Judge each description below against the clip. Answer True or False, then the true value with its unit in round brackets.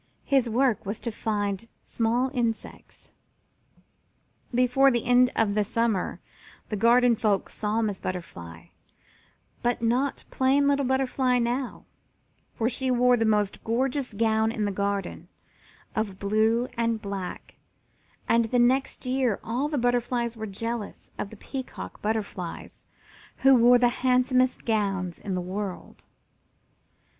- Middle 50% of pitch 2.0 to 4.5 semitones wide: True (3.1 semitones)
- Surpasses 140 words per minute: False (135 wpm)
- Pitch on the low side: False (230 Hz)